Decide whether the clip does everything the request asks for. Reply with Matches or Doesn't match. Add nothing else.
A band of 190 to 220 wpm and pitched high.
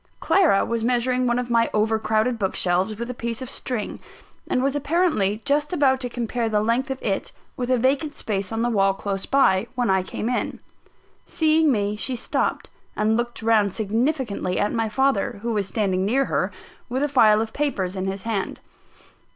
Matches